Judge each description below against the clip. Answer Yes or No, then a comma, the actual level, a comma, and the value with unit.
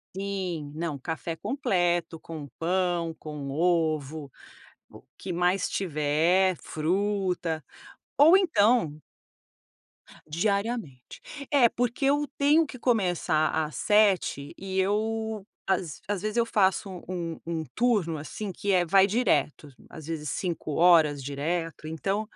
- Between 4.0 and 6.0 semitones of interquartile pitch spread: Yes, average, 4.6 semitones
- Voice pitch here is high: No, medium, 180 Hz